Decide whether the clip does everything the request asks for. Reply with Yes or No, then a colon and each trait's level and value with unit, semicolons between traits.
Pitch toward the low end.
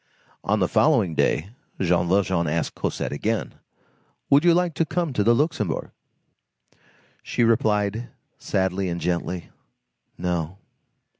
Yes: low, 100 Hz